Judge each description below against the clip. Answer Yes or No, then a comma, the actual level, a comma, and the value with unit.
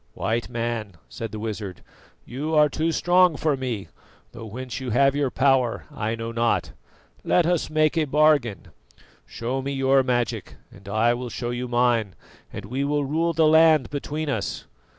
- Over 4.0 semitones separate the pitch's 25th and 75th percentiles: Yes, average, 4.5 semitones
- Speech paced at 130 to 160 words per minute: No, average, 170 wpm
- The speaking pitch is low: Yes, low, 130 Hz